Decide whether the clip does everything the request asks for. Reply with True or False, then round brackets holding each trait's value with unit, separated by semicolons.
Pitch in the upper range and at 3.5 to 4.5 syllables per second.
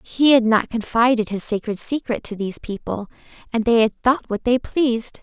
False (230 Hz; 5.1 syllables/s)